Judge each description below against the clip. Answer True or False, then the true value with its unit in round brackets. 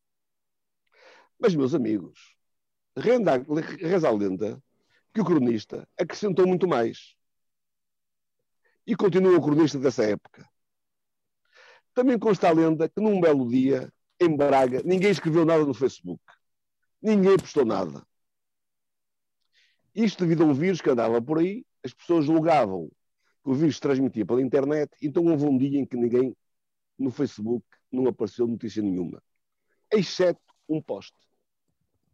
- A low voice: False (160 Hz)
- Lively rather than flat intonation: True (6.7 semitones)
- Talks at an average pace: True (135 wpm)